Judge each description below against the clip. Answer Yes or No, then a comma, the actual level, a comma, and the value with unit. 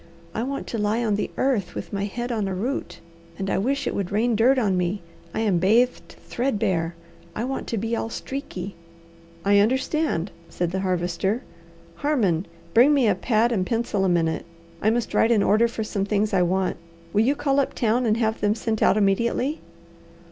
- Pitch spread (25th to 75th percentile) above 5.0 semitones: No, average, 3.7 semitones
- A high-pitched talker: Yes, high, 215 Hz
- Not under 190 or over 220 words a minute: Yes, average, 200 wpm